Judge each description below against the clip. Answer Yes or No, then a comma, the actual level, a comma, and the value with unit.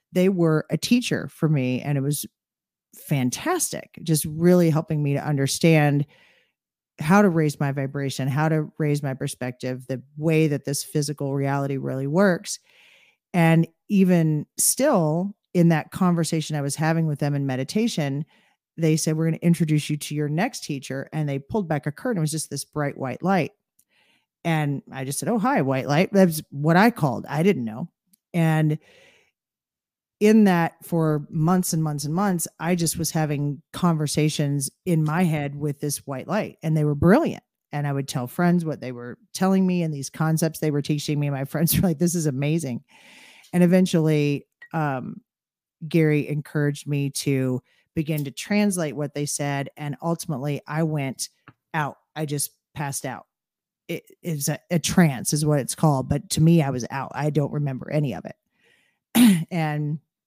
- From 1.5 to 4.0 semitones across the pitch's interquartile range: Yes, average, 3.2 semitones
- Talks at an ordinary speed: Yes, average, 180 wpm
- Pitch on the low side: No, medium, 155 Hz